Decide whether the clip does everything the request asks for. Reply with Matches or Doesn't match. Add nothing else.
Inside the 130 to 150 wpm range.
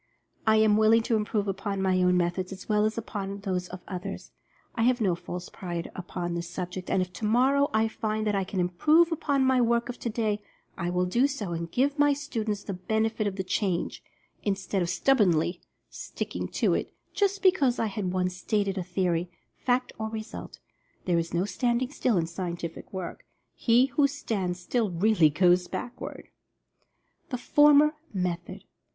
Doesn't match